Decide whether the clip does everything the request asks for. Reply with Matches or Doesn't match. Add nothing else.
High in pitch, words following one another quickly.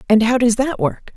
Matches